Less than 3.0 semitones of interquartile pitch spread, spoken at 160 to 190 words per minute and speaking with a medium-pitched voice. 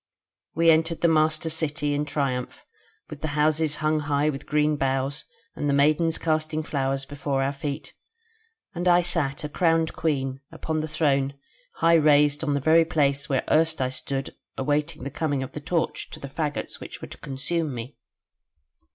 Yes: narrow, 2.4 semitones; average, 175 wpm; medium, 150 Hz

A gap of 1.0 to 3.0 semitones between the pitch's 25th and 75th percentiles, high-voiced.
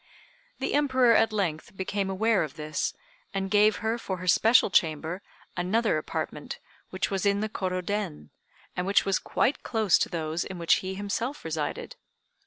No: average, 3.9 semitones; high, 195 Hz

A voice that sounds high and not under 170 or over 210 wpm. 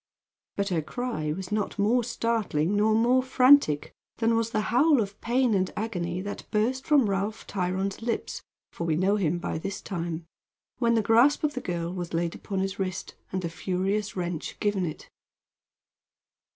Yes: high, 200 Hz; average, 175 wpm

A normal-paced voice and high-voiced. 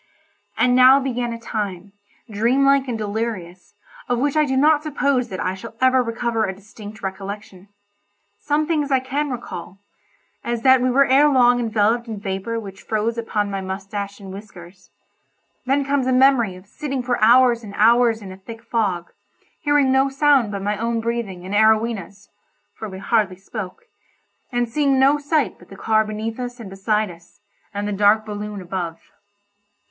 Yes: average, 175 wpm; high, 225 Hz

